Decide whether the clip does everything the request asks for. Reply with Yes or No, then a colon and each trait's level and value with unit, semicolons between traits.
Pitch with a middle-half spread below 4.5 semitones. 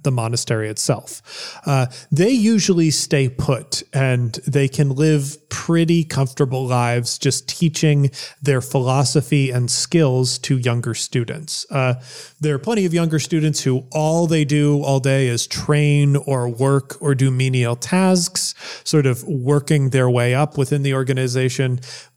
Yes: average, 2.9 semitones